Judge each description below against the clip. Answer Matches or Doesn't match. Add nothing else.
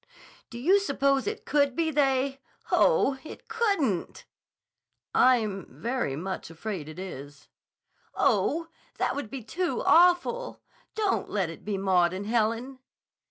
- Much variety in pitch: Matches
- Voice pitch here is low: Doesn't match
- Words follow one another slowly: Matches